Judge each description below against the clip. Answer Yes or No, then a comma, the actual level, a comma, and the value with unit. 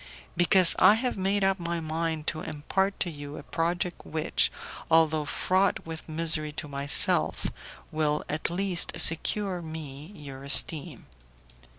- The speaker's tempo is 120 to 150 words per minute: Yes, average, 140 wpm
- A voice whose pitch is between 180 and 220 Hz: No, medium, 165 Hz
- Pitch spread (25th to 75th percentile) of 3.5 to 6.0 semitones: No, average, 3.0 semitones